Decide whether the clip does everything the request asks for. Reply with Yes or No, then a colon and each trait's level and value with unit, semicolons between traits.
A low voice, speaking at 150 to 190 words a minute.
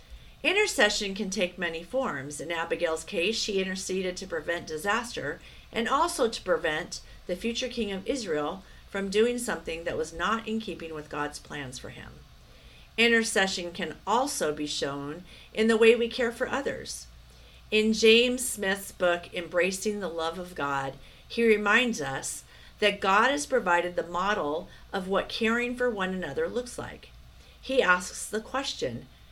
No: high, 195 Hz; average, 160 wpm